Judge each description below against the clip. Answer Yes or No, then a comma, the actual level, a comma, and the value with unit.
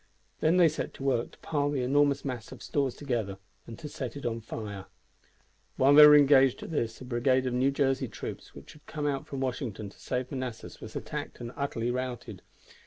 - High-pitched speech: No, low, 130 Hz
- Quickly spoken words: Yes, fast, 210 wpm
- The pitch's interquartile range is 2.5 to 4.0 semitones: Yes, average, 3.0 semitones